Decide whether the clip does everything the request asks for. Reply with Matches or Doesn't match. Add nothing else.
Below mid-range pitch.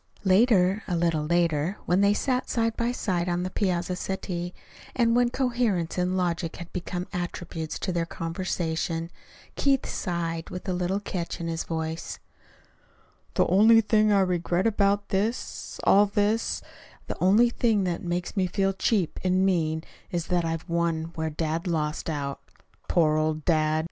Doesn't match